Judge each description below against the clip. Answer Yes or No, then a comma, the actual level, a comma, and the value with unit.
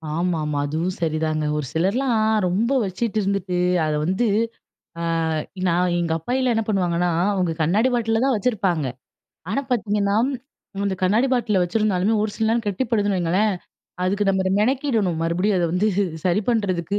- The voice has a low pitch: No, high, 195 Hz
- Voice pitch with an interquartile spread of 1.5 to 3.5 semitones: No, average, 4.0 semitones